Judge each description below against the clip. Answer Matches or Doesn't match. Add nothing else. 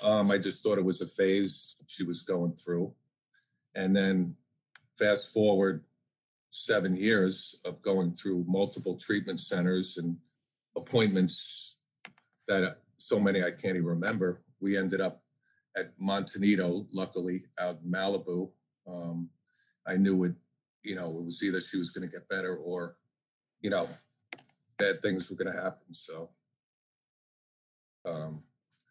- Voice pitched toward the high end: Doesn't match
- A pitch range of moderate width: Doesn't match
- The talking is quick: Doesn't match